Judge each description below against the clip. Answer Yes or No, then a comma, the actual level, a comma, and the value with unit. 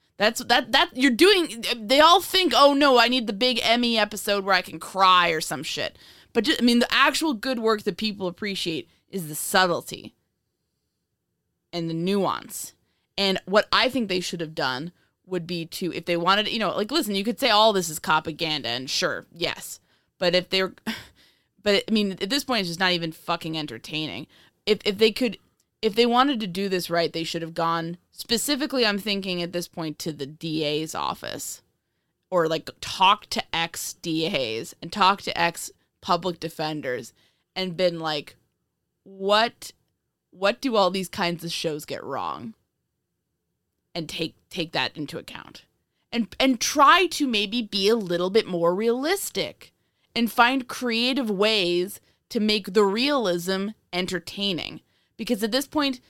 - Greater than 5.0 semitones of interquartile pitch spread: Yes, wide, 5.6 semitones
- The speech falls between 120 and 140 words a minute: No, average, 175 wpm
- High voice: Yes, high, 195 Hz